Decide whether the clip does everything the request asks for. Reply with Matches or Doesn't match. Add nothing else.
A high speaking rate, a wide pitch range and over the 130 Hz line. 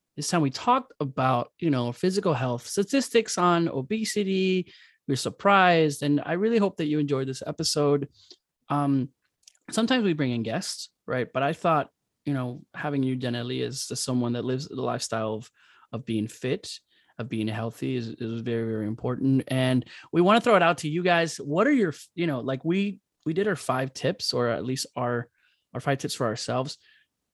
Doesn't match